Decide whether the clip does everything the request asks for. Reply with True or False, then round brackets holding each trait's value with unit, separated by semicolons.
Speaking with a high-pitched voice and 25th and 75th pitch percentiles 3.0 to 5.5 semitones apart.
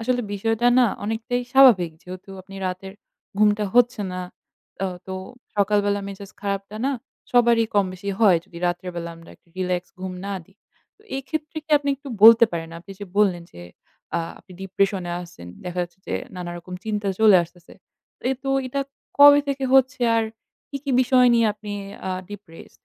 True (205 Hz; 4.5 semitones)